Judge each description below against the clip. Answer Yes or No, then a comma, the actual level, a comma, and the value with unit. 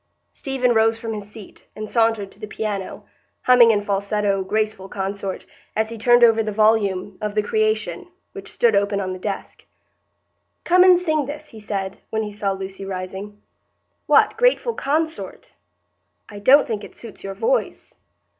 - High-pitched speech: Yes, high, 215 Hz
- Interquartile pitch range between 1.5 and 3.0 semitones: Yes, average, 2.7 semitones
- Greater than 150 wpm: Yes, average, 165 wpm